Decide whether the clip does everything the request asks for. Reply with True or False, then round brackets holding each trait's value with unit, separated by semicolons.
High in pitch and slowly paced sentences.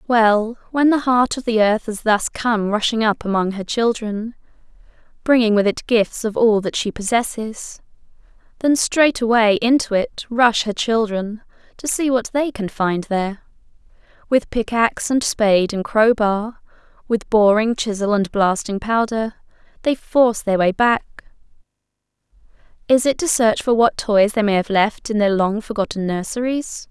False (220 Hz; 160 wpm)